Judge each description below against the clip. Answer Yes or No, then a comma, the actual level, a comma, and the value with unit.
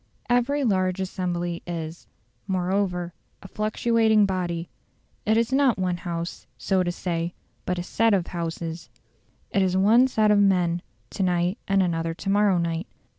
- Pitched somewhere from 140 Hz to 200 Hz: Yes, medium, 185 Hz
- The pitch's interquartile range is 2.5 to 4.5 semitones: Yes, average, 3.2 semitones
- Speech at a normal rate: Yes, average, 155 wpm